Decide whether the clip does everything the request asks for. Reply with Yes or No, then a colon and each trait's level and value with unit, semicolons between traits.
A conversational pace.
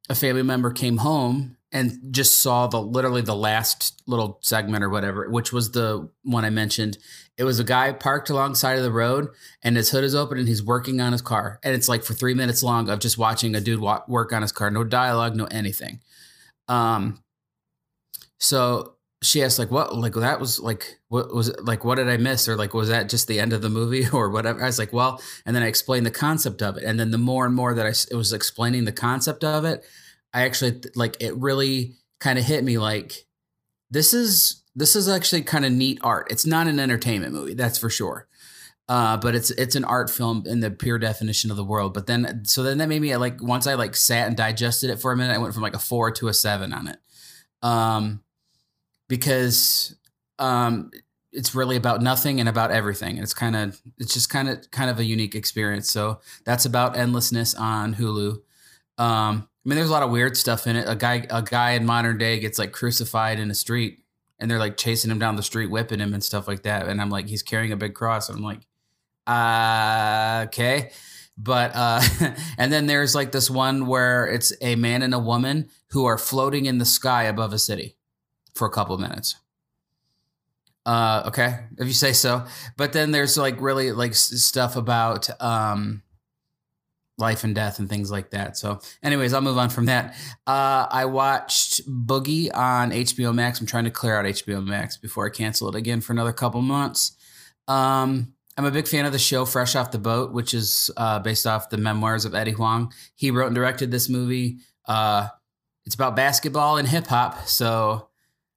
No: fast, 215 wpm